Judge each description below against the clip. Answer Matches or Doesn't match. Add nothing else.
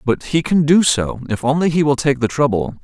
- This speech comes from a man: Matches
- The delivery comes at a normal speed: Doesn't match